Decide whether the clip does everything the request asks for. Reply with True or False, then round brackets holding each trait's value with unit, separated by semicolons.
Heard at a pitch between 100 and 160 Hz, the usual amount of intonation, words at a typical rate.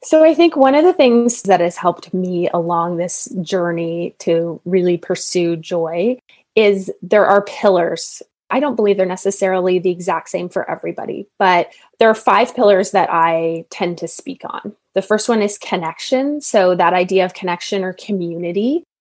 False (185 Hz; 3.6 semitones; 175 wpm)